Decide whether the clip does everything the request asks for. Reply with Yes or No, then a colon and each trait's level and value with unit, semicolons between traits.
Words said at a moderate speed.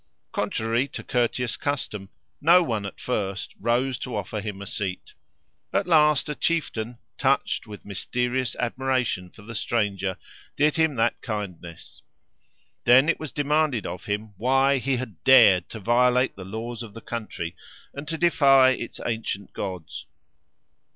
Yes: average, 150 wpm